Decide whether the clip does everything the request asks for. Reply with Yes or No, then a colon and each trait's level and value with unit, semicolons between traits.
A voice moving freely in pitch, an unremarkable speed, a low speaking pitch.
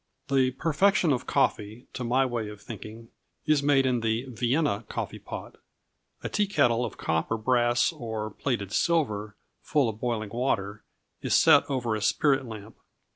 No: average, 3.8 semitones; average, 160 wpm; low, 120 Hz